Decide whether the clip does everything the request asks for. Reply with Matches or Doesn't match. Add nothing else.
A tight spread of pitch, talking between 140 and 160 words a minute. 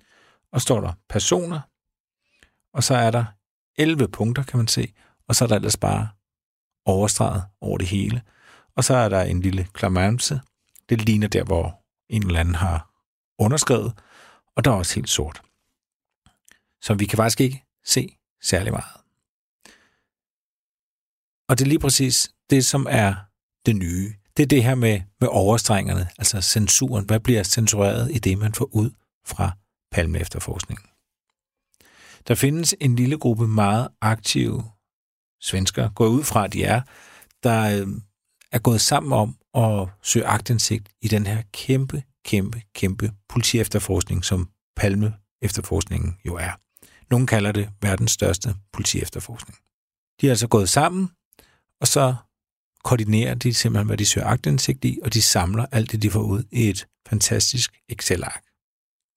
Doesn't match